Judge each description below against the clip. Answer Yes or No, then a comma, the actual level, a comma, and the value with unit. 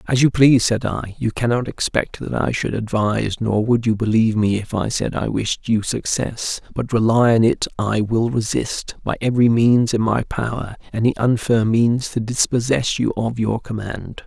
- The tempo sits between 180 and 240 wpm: Yes, average, 195 wpm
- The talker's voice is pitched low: Yes, low, 115 Hz